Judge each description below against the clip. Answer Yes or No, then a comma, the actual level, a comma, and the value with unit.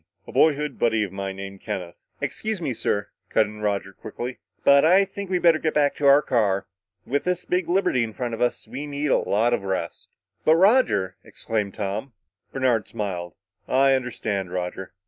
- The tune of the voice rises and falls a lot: Yes, wide, 6.8 semitones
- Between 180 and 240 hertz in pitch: No, low, 120 Hz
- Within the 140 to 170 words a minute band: No, average, 190 wpm